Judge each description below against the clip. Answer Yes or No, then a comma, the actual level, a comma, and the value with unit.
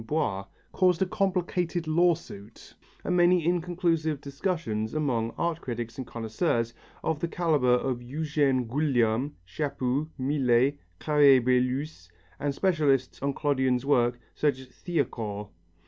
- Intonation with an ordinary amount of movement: Yes, average, 4.8 semitones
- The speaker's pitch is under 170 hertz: Yes, medium, 140 Hz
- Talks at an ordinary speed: No, slow, 120 wpm